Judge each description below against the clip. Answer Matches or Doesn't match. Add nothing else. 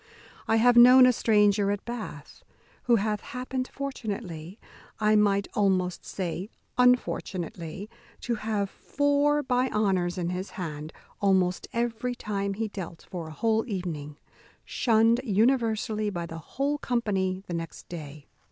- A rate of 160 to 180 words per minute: Doesn't match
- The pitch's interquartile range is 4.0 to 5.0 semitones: Matches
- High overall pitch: Matches